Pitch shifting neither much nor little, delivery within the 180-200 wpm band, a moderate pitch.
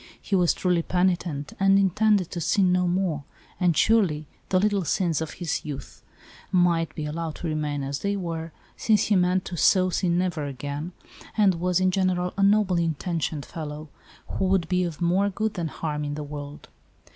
Yes: average, 3.3 semitones; average, 185 wpm; medium, 175 Hz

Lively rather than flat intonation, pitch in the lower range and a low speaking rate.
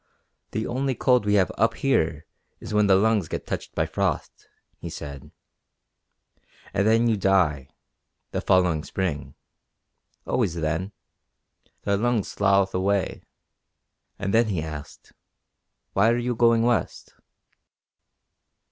No: average, 4.8 semitones; low, 100 Hz; slow, 125 wpm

